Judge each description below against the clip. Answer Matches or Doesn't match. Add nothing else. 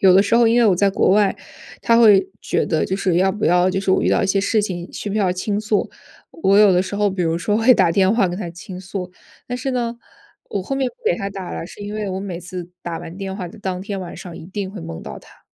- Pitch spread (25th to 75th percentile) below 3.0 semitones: Matches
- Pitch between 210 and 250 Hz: Doesn't match